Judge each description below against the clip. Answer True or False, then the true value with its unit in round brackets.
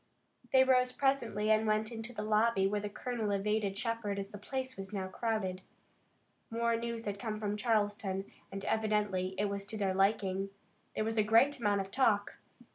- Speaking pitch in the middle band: False (210 Hz)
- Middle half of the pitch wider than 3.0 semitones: False (2.4 semitones)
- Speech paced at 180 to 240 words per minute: True (185 wpm)